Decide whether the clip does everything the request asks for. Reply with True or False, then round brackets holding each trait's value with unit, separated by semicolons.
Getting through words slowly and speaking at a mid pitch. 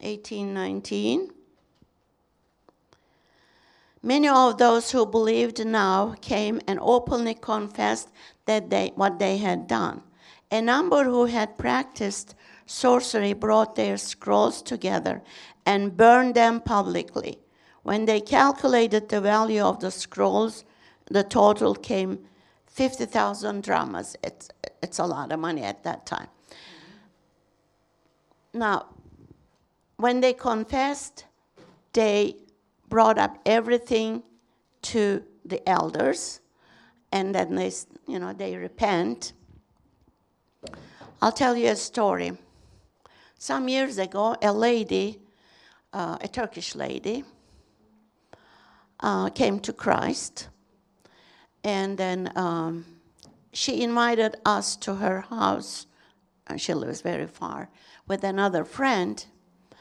False (110 wpm; 210 Hz)